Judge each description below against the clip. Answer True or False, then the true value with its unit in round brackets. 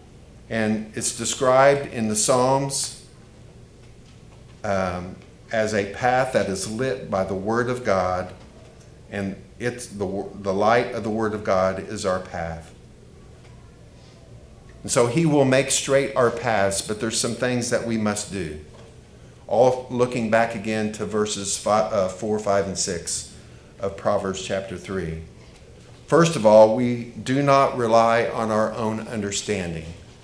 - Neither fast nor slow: True (145 wpm)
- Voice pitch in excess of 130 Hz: False (110 Hz)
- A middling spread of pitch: True (3.8 semitones)